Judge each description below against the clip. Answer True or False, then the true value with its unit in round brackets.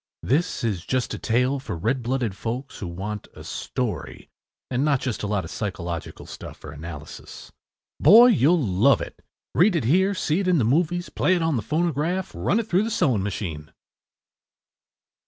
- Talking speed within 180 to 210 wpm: True (185 wpm)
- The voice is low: True (130 Hz)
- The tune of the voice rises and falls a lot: True (8.8 semitones)